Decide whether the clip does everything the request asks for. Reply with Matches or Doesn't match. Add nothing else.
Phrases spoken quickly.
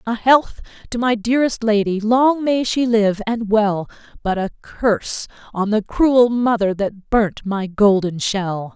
Doesn't match